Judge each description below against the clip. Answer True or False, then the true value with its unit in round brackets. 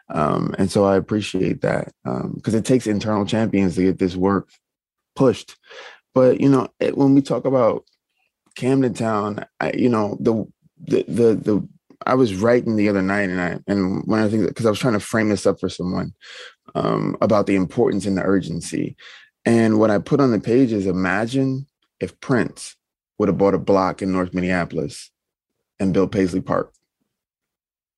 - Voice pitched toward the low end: True (105 Hz)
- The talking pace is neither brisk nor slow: True (180 wpm)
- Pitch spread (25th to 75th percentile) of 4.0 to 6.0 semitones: False (3.4 semitones)